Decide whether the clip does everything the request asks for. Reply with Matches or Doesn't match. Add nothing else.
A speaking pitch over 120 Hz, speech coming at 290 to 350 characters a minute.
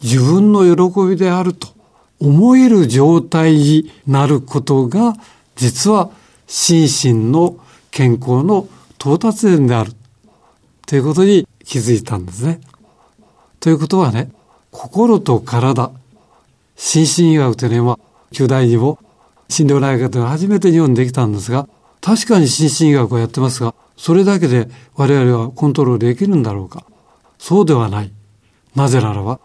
Doesn't match